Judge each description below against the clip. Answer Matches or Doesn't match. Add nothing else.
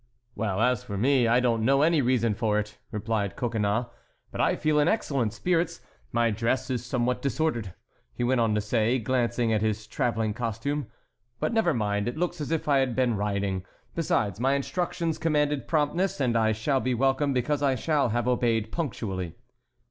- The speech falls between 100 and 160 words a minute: Doesn't match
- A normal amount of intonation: Matches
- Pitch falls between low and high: Doesn't match